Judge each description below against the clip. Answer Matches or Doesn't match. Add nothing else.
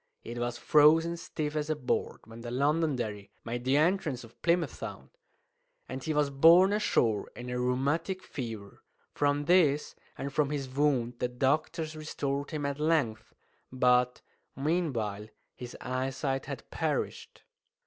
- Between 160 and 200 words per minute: Doesn't match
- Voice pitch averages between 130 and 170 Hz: Matches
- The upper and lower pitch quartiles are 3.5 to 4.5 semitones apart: Matches